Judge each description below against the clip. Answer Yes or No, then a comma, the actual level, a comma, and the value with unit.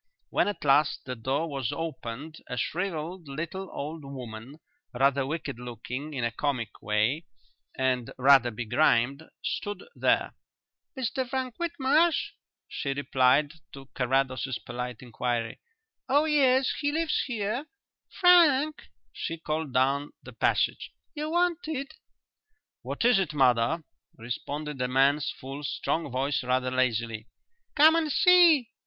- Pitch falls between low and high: Yes, medium, 145 Hz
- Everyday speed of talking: No, slow, 125 wpm